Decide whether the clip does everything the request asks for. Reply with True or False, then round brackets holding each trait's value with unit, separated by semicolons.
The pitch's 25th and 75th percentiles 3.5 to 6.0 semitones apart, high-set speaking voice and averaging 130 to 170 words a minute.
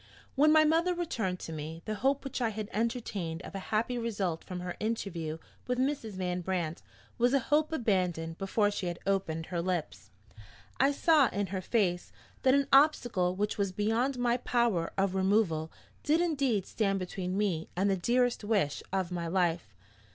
False (5.5 semitones; 200 Hz; 180 wpm)